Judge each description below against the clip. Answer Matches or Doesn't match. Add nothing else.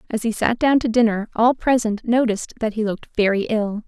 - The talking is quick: Matches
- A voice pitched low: Doesn't match